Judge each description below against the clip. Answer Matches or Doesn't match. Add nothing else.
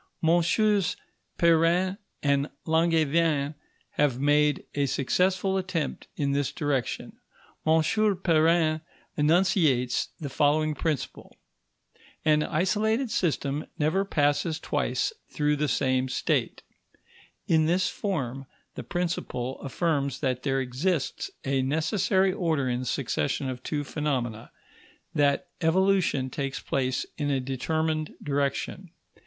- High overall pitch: Doesn't match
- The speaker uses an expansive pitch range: Doesn't match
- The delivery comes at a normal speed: Doesn't match